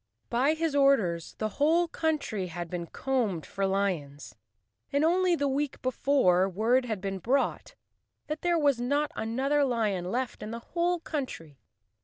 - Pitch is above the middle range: Yes, very high, 255 Hz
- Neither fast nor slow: Yes, average, 155 wpm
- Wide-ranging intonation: Yes, wide, 7.1 semitones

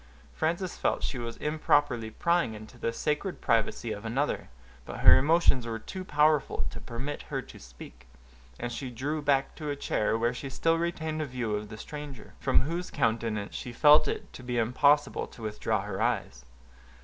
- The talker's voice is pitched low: Yes, low, 130 Hz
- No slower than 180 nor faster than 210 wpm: Yes, average, 185 wpm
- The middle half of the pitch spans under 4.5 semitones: No, average, 4.8 semitones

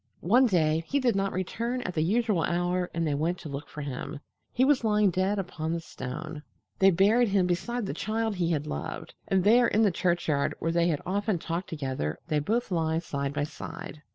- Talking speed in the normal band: No, fast, 210 wpm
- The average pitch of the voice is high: No, medium, 175 Hz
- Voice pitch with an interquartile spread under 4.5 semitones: No, average, 4.8 semitones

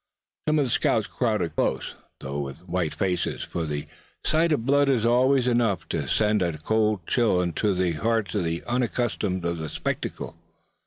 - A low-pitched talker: Yes, low, 105 Hz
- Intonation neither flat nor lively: No, wide, 5.8 semitones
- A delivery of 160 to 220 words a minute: Yes, average, 175 wpm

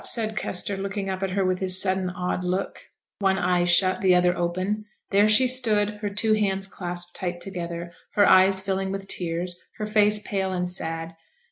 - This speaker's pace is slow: No, average, 190 wpm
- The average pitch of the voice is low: No, high, 190 Hz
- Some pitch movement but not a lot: No, narrow, 2.1 semitones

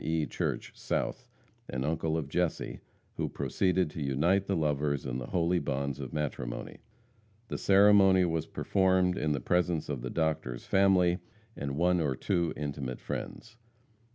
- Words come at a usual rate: Yes, average, 155 wpm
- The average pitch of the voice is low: Yes, very low, 80 Hz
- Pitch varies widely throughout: No, average, 4.3 semitones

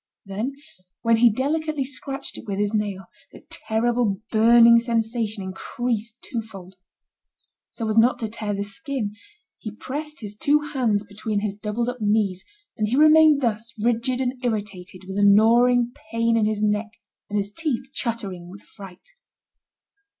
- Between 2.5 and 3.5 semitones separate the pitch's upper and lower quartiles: Yes, average, 3.0 semitones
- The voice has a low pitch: No, high, 225 Hz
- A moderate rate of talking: Yes, average, 155 wpm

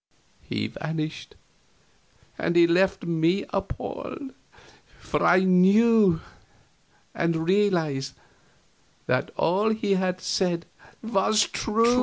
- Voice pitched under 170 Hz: No, medium, 185 Hz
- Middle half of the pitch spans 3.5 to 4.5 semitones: Yes, average, 3.8 semitones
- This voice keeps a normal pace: No, slow, 90 wpm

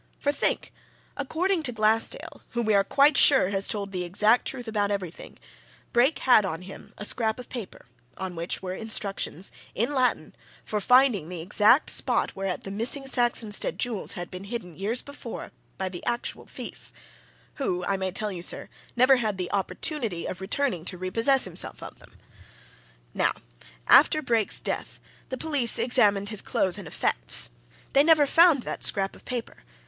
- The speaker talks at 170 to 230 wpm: Yes, average, 175 wpm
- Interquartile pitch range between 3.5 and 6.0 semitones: Yes, average, 5.0 semitones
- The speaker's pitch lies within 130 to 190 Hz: No, high, 215 Hz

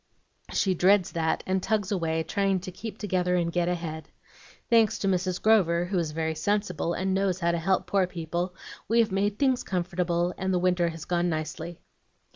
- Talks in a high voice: No, medium, 180 Hz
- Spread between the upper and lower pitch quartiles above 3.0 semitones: No, narrow, 2.4 semitones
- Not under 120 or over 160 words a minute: No, average, 190 wpm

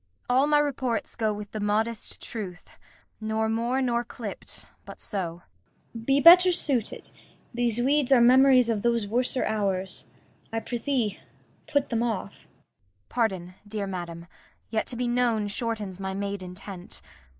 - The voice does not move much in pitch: No, average, 3.5 semitones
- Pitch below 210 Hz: No, high, 225 Hz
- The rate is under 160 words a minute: Yes, average, 150 wpm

